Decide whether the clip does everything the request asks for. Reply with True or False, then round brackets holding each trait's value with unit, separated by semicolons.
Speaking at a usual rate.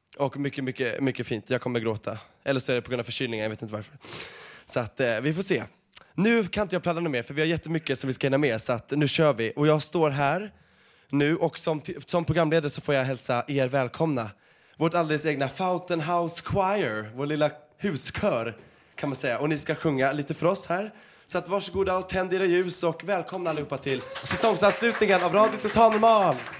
False (225 wpm)